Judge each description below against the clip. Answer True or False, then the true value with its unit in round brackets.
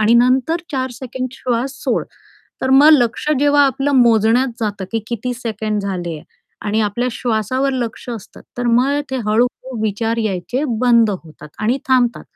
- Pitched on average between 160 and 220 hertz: False (235 Hz)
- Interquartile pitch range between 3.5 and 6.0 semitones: False (3.1 semitones)